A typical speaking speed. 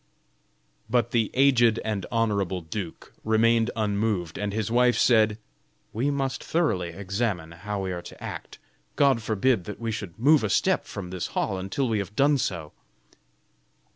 Yes: average, 160 wpm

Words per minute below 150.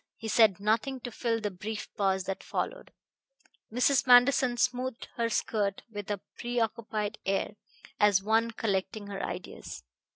Yes: average, 140 wpm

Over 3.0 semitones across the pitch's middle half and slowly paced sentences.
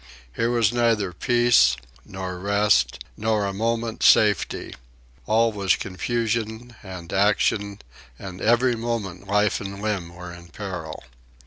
Yes: average, 3.6 semitones; slow, 125 wpm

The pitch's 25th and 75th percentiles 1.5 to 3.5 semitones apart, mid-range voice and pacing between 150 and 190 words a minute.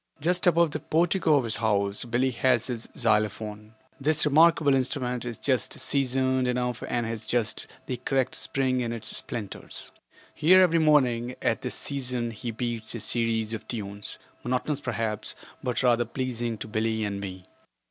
No: average, 3.2 semitones; low, 120 Hz; average, 160 wpm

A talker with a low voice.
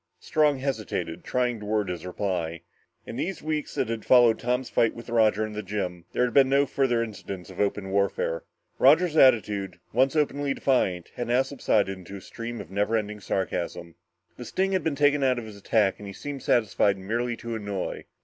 Yes: low, 110 Hz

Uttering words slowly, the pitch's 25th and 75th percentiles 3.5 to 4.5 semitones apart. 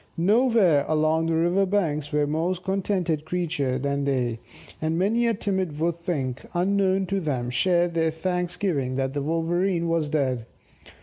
No: average, 150 wpm; average, 4.2 semitones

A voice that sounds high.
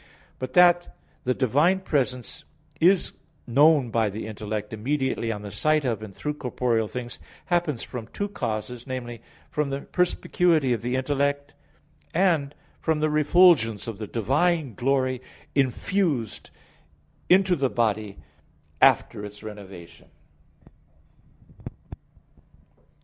No: low, 130 Hz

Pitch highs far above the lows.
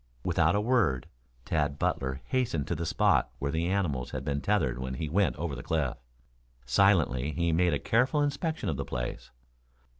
Yes: wide, 6.6 semitones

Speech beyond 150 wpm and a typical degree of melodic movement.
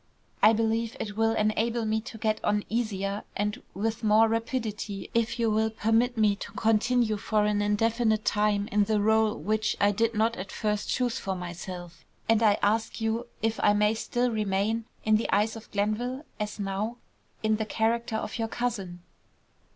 No: average, 180 wpm; narrow, 1.5 semitones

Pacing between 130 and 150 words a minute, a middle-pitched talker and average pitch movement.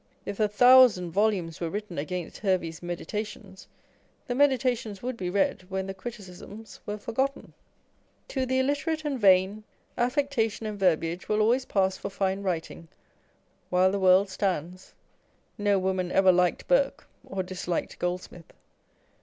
No: average, 145 wpm; high, 195 Hz; average, 3.6 semitones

